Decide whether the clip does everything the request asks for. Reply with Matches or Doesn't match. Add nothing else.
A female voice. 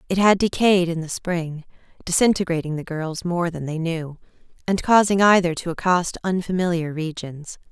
Matches